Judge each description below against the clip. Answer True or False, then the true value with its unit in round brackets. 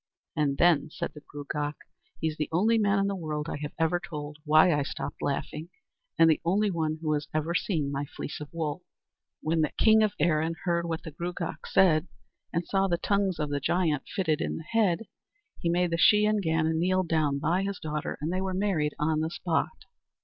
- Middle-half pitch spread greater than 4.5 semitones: False (3.3 semitones)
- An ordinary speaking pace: False (215 wpm)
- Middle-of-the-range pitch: True (165 Hz)